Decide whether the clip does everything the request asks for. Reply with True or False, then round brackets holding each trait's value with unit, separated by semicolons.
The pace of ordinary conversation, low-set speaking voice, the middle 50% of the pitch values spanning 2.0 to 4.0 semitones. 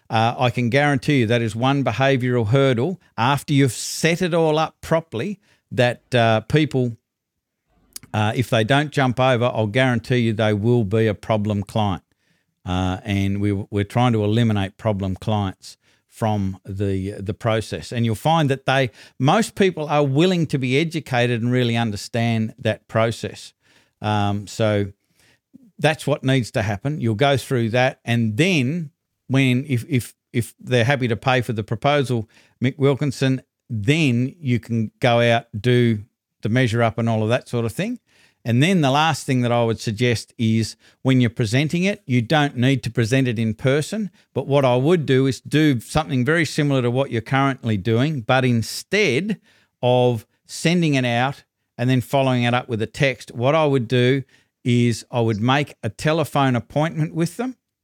True (175 wpm; 125 Hz; 3.7 semitones)